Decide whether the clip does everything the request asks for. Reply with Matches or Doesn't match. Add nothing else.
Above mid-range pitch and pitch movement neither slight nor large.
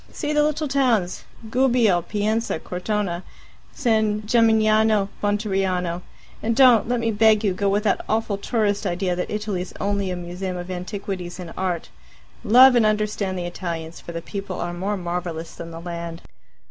Matches